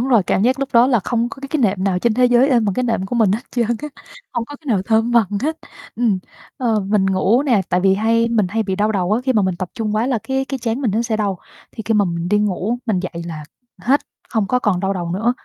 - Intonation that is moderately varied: Yes, average, 3.9 semitones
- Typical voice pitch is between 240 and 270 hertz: No, high, 220 Hz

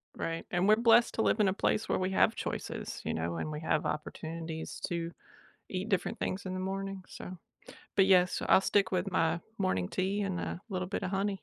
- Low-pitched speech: No, medium, 185 Hz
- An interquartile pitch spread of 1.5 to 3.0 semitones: Yes, average, 2.7 semitones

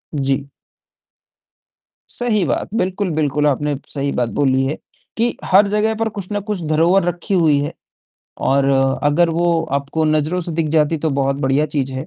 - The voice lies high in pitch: No, medium, 155 Hz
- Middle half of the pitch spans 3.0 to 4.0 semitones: No, average, 4.5 semitones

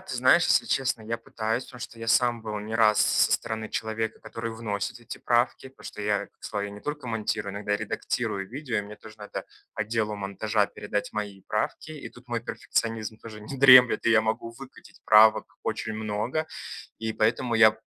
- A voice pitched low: Yes, low, 110 Hz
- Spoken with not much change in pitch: Yes, narrow, 1.9 semitones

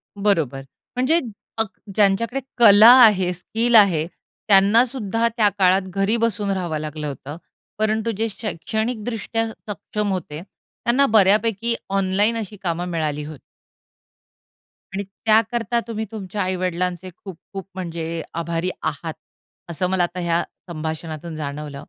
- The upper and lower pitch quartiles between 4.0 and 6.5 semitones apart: Yes, average, 4.6 semitones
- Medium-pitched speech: No, high, 195 Hz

